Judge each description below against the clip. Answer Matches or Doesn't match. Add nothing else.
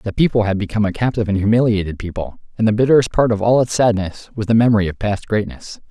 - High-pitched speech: Doesn't match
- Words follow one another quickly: Matches